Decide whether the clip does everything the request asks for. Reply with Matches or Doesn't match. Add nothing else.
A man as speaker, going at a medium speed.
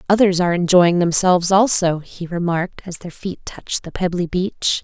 Doesn't match